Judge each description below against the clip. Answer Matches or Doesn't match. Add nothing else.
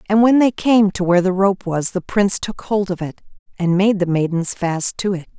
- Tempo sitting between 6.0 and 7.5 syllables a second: Doesn't match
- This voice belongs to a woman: Matches